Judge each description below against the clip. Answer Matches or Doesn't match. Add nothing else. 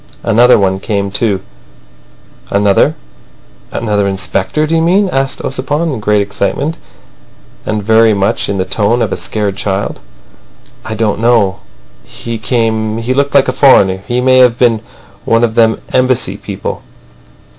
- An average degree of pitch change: Matches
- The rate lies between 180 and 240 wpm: Doesn't match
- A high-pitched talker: Doesn't match